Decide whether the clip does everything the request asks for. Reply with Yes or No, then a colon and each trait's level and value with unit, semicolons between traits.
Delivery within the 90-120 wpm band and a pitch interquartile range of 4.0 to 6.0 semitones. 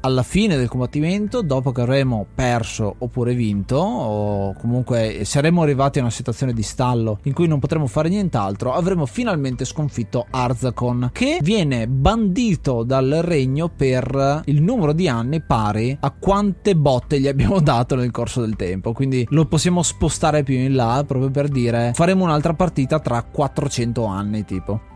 No: average, 160 wpm; average, 4.6 semitones